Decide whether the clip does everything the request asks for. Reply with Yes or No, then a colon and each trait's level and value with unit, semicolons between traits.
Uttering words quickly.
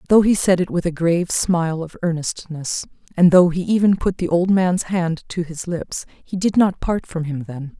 Yes: fast, 225 wpm